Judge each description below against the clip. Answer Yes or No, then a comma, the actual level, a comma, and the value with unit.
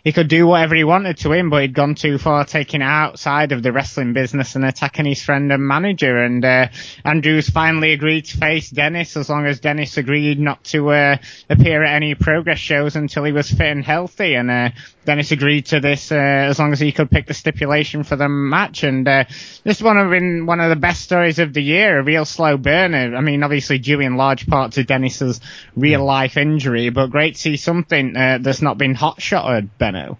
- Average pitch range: No, narrow, 2.3 semitones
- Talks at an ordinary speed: No, fast, 220 wpm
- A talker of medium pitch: Yes, medium, 145 Hz